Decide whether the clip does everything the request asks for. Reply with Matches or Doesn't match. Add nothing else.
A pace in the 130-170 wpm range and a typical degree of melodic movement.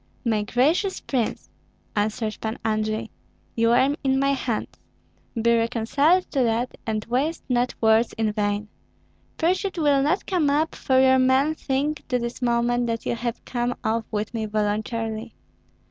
Matches